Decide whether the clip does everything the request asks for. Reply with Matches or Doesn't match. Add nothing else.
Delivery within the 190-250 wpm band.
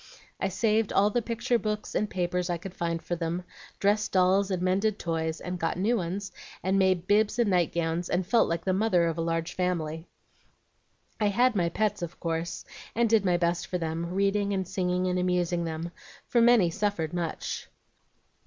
Matches